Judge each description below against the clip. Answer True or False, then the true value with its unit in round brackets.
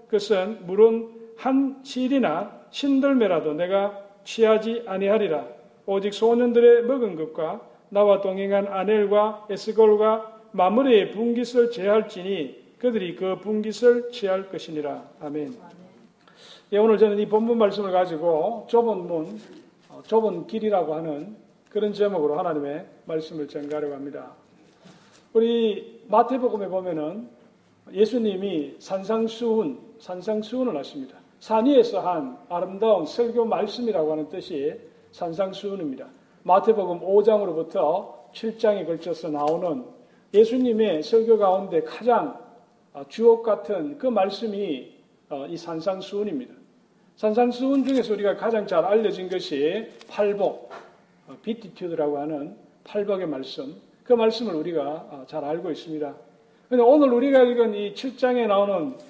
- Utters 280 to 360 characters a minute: True (285 characters per minute)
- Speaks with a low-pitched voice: False (210 Hz)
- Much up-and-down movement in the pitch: False (4.1 semitones)